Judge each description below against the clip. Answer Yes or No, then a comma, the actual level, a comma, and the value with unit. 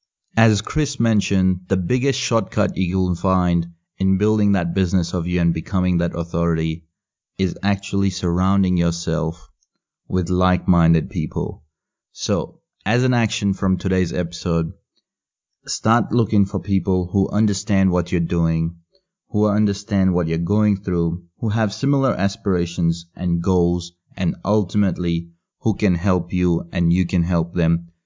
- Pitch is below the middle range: Yes, very low, 95 Hz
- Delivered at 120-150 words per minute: Yes, average, 140 wpm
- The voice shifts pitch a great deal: No, average, 3.0 semitones